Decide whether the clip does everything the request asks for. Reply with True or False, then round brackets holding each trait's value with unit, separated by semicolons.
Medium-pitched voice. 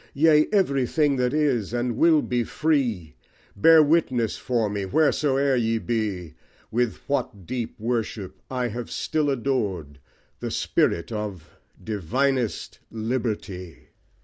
False (120 Hz)